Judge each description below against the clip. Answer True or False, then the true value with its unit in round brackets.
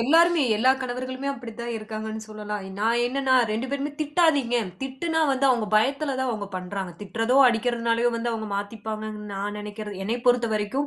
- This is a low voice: False (235 Hz)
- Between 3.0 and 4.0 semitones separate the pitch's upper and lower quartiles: True (3.6 semitones)